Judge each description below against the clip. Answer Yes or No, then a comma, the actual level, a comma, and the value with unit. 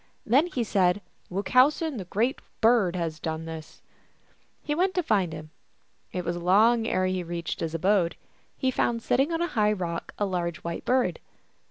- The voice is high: Yes, high, 195 Hz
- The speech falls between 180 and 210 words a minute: Yes, average, 185 wpm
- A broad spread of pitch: Yes, wide, 6.1 semitones